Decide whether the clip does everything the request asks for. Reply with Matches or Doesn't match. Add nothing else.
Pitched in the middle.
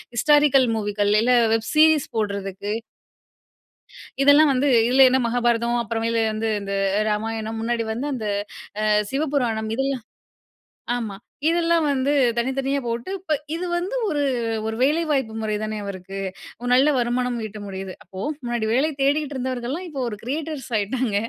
Doesn't match